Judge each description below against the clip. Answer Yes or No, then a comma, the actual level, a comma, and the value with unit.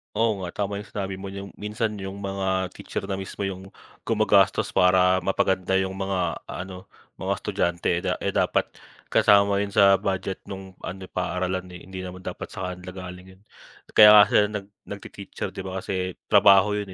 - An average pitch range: No, narrow, 1.3 semitones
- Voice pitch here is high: No, very low, 95 Hz